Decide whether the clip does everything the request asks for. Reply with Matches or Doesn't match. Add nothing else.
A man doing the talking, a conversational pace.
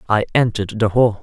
Matches